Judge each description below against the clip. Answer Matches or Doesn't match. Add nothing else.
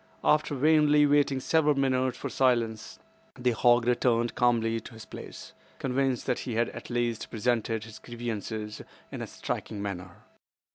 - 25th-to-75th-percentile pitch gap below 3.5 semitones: Matches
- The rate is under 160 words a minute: Matches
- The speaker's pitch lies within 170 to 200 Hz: Doesn't match